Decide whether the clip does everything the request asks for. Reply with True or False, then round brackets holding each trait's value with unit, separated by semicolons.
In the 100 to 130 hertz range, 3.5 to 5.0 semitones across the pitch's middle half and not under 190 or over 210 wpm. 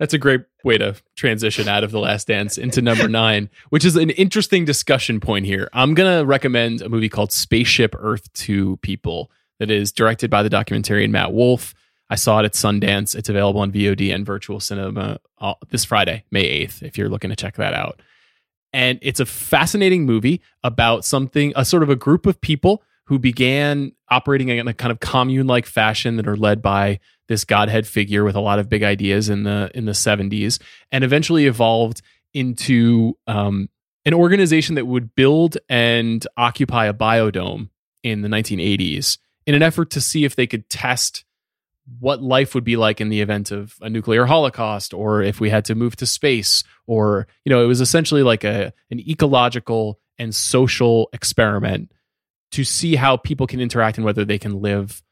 True (115 Hz; 4.3 semitones; 195 wpm)